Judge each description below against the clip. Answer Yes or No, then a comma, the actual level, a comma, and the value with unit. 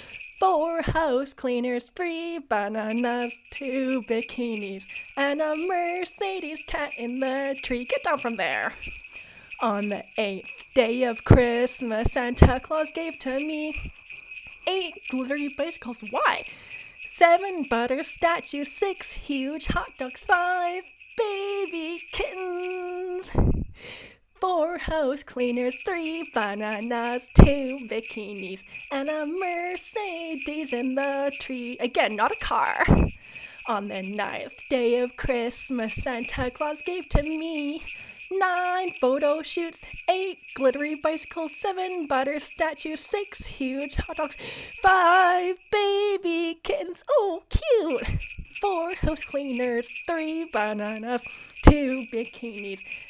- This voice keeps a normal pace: No, slow, 110 wpm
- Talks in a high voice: Yes, very high, 295 Hz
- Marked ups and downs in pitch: Yes, wide, 5.9 semitones